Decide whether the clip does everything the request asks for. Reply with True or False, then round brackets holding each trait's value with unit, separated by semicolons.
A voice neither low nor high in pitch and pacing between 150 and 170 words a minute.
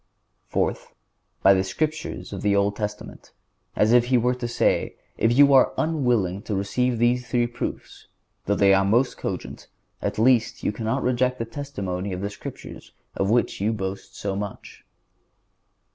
False (115 Hz; 160 wpm)